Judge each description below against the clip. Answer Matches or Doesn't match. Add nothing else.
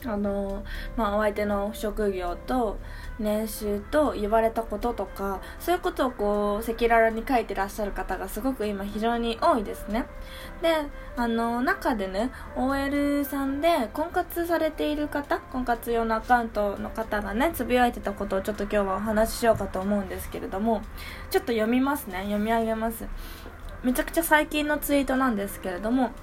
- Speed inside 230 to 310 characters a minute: Doesn't match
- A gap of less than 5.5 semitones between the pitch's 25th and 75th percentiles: Matches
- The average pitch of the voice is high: Matches